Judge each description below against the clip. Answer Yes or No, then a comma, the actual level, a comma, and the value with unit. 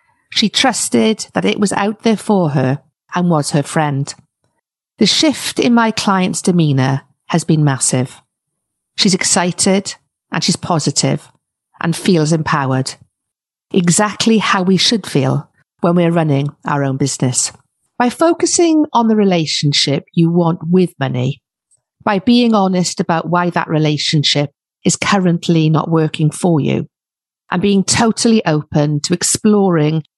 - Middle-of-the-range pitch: Yes, medium, 170 Hz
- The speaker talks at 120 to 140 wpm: Yes, slow, 135 wpm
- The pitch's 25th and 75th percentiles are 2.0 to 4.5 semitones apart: No, average, 5.3 semitones